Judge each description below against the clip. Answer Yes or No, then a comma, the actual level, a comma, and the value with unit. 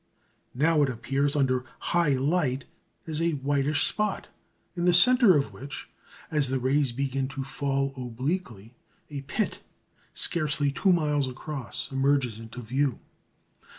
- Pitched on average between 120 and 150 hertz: Yes, medium, 140 Hz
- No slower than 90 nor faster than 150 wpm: Yes, slow, 135 wpm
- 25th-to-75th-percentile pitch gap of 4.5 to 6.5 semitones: No, narrow, 2.6 semitones